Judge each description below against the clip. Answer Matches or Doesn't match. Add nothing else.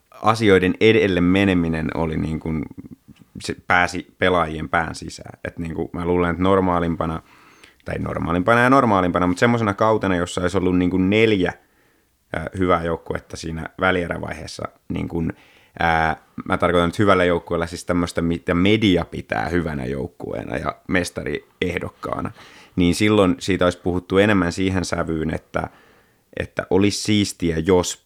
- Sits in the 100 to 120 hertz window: Doesn't match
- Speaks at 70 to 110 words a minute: Doesn't match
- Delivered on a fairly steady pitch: Matches